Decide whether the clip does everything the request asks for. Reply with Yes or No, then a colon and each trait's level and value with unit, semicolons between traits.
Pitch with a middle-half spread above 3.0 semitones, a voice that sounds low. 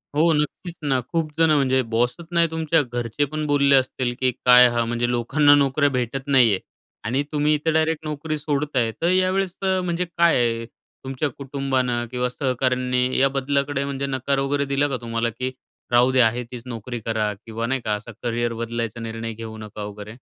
Yes: average, 3.5 semitones; low, 130 Hz